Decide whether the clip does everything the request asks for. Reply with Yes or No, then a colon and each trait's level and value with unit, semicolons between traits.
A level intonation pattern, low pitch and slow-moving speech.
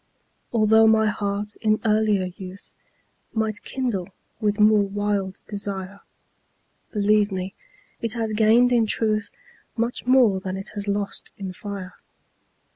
No: narrow, 1.6 semitones; high, 210 Hz; slow, 125 wpm